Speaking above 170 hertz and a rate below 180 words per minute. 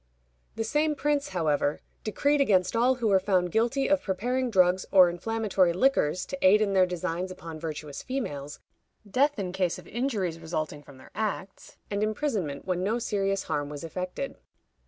Yes: high, 190 Hz; average, 170 wpm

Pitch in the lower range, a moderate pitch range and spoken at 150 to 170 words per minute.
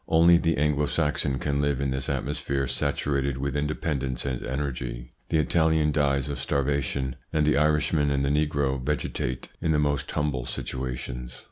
No: very low, 70 Hz; narrow, 2.1 semitones; average, 160 wpm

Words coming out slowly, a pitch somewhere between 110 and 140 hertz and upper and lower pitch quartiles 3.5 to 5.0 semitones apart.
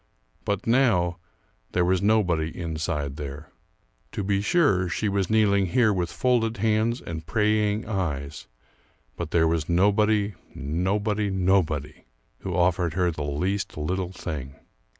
No: slow, 130 wpm; very low, 95 Hz; average, 4.4 semitones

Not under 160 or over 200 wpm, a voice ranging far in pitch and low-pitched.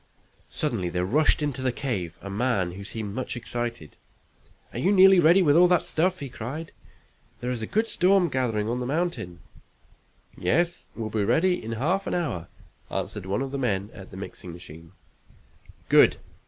Yes: average, 170 wpm; wide, 8.5 semitones; low, 125 Hz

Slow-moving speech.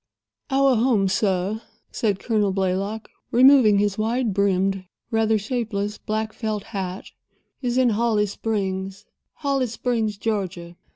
Yes: slow, 115 wpm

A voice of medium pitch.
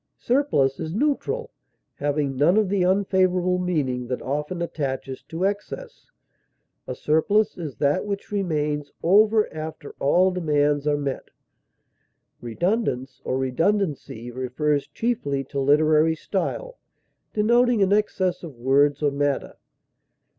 Yes: medium, 155 Hz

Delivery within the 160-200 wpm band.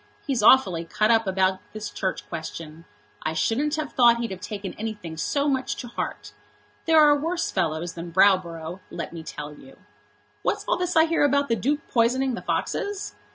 Yes: average, 185 wpm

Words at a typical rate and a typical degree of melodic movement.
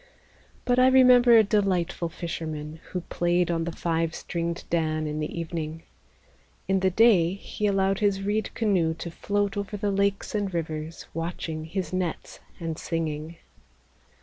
Yes: average, 150 wpm; average, 3.6 semitones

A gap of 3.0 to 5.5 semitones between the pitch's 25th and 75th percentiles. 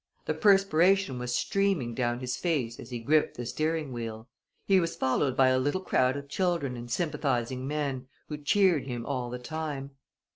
Yes: average, 4.5 semitones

